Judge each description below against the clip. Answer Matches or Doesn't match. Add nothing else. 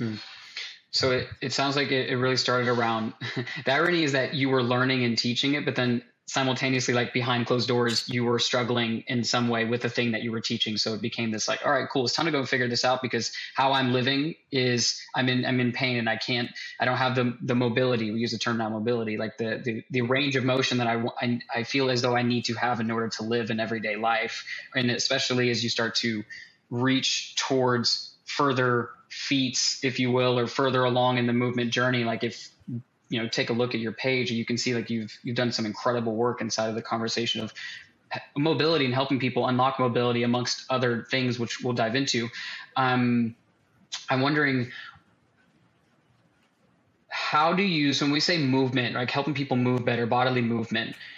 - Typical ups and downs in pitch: Doesn't match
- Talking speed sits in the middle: Doesn't match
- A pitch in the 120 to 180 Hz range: Matches